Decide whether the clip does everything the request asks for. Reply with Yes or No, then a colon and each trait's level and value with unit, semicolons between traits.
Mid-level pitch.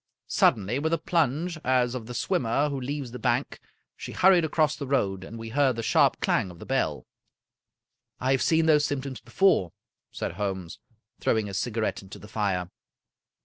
No: low, 125 Hz